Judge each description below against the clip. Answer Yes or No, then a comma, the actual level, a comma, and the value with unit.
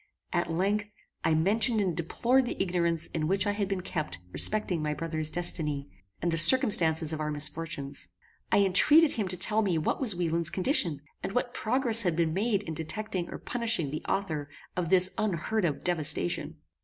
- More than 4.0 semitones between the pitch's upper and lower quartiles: Yes, average, 4.5 semitones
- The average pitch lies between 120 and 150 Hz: No, medium, 175 Hz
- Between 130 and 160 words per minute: No, average, 180 wpm